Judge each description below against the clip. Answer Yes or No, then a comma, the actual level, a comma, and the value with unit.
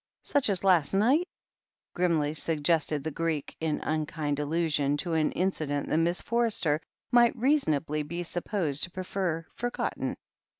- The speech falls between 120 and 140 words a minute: Yes, slow, 135 wpm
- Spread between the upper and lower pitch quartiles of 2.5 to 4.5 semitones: Yes, average, 4.1 semitones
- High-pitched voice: No, medium, 165 Hz